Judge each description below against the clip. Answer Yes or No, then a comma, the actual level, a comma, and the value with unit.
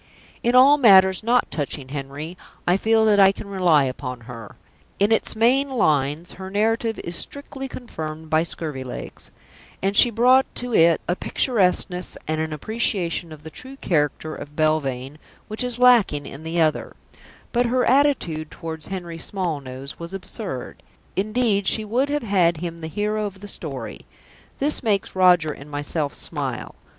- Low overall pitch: No, medium, 180 Hz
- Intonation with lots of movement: Yes, wide, 6.4 semitones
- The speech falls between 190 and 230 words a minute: No, average, 160 wpm